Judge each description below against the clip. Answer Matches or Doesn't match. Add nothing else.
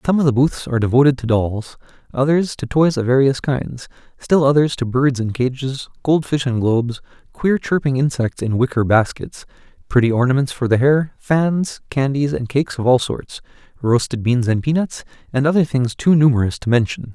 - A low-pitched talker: Matches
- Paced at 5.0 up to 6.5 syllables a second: Matches